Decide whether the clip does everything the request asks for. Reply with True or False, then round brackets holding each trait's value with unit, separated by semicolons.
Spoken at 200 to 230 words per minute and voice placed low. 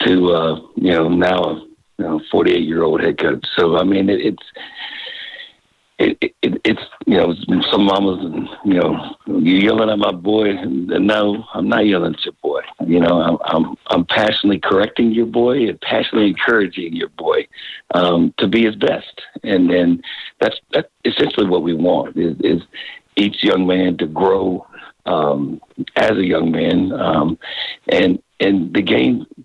False (175 wpm; 115 Hz)